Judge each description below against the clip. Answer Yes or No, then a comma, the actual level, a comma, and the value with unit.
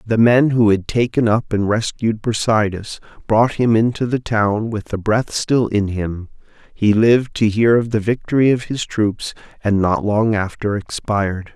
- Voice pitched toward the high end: No, low, 110 Hz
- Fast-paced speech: No, average, 180 wpm